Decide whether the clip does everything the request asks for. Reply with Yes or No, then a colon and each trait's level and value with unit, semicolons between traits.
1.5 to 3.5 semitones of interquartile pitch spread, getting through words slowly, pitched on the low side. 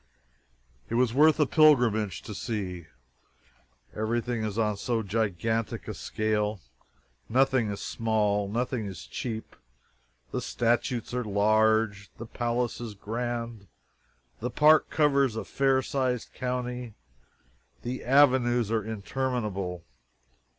Yes: average, 2.8 semitones; slow, 115 wpm; low, 115 Hz